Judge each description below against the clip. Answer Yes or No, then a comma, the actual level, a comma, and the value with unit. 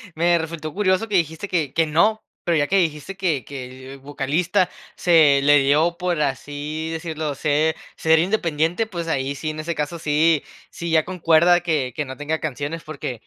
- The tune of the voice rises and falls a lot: No, average, 2.7 semitones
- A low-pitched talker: No, medium, 160 Hz